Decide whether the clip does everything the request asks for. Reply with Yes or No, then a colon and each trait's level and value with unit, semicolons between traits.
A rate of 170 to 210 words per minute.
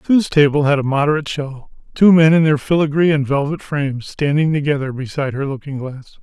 Yes: average, 195 wpm